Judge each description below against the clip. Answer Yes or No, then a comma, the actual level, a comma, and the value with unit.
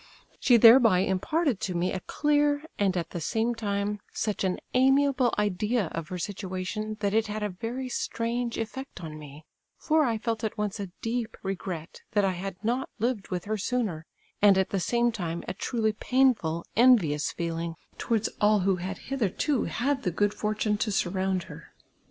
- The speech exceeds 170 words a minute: Yes, average, 180 wpm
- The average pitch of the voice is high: Yes, high, 210 Hz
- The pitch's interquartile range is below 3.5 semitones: No, average, 4.3 semitones